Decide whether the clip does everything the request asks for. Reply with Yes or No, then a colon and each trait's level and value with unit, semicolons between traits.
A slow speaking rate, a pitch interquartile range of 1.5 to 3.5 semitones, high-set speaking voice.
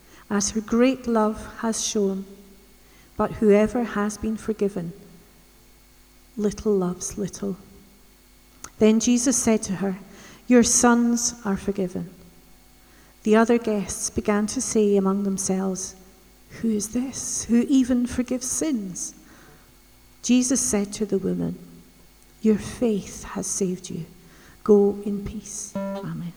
Yes: slow, 120 wpm; average, 2.9 semitones; high, 205 Hz